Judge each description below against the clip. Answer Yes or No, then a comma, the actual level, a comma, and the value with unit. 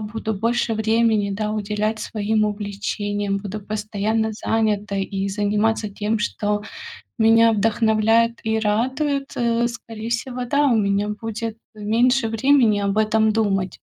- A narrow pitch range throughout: Yes, narrow, 1.6 semitones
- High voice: Yes, high, 220 Hz